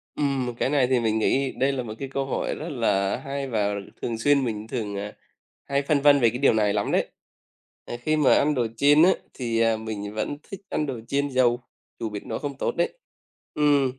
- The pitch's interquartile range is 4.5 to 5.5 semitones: No, average, 4.1 semitones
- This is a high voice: No, low, 130 Hz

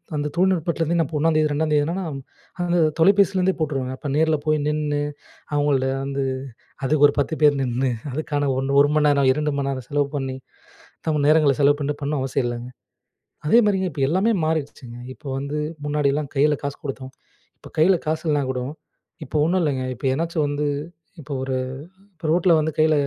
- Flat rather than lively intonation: Yes, narrow, 2.3 semitones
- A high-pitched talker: No, medium, 150 Hz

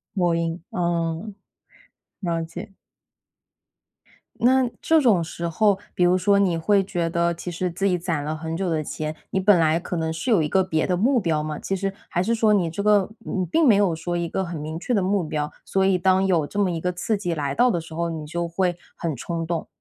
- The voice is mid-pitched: Yes, medium, 175 Hz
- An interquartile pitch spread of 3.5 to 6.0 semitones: No, average, 3.0 semitones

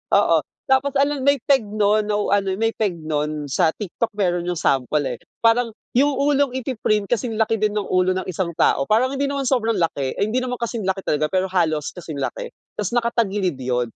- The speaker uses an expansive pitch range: Yes, wide, 5.8 semitones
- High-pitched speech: Yes, high, 210 Hz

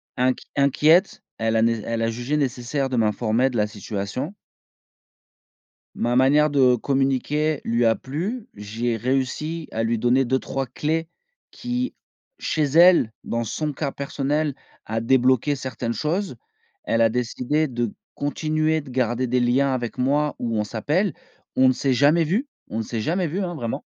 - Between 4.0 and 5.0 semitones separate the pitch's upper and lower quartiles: Yes, average, 4.4 semitones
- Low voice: Yes, low, 130 Hz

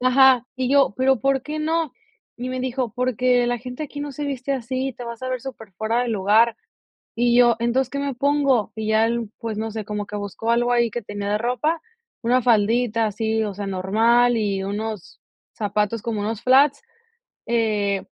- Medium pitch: No, high, 235 Hz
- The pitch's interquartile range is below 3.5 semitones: Yes, average, 3.0 semitones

